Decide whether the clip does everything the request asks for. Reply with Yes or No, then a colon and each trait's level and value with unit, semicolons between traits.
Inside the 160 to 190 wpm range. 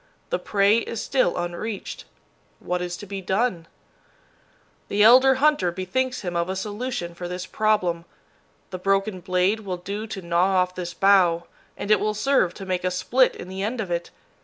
Yes: average, 185 wpm